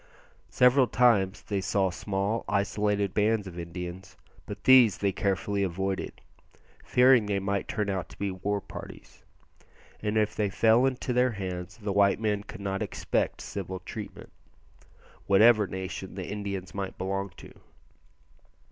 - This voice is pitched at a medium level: No, low, 100 Hz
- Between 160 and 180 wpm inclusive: No, average, 145 wpm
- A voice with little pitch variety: Yes, narrow, 1.9 semitones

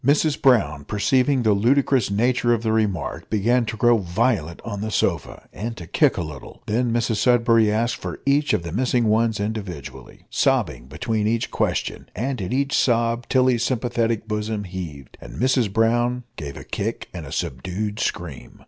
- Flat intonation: No, average, 3.4 semitones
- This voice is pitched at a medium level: No, low, 115 Hz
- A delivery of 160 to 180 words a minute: Yes, average, 175 wpm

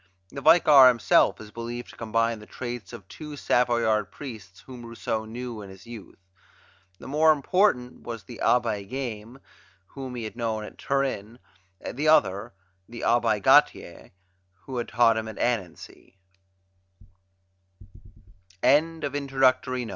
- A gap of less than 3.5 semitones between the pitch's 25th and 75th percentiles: Yes, average, 2.7 semitones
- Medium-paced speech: No, slow, 130 wpm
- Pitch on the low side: Yes, low, 120 Hz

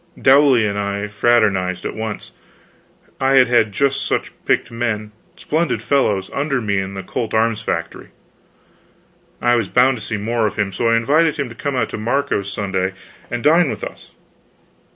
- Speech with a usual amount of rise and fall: Yes, average, 4.5 semitones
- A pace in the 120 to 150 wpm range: No, average, 175 wpm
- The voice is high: No, low, 115 Hz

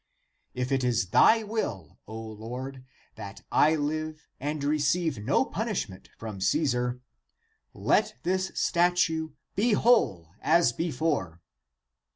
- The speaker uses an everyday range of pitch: No, wide, 6.6 semitones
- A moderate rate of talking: No, slow, 115 wpm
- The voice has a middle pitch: Yes, medium, 145 Hz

